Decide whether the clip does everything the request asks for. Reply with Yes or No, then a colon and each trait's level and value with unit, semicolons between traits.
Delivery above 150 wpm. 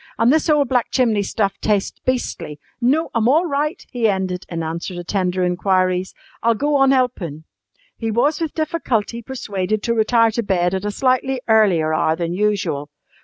Yes: average, 175 wpm